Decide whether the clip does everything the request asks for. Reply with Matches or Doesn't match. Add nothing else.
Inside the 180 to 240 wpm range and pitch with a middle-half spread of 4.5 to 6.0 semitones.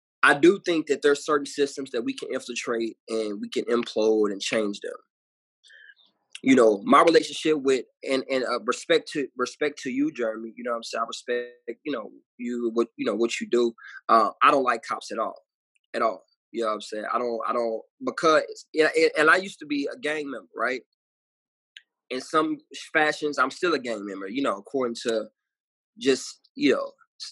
Matches